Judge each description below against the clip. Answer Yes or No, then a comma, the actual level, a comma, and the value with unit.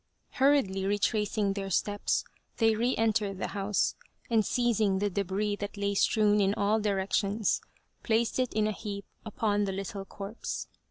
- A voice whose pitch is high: Yes, high, 205 Hz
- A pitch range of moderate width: No, narrow, 1.7 semitones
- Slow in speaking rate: No, average, 155 wpm